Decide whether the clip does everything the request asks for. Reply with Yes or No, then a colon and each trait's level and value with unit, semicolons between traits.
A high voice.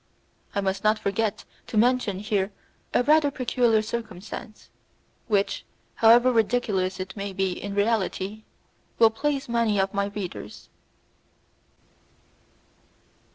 Yes: high, 215 Hz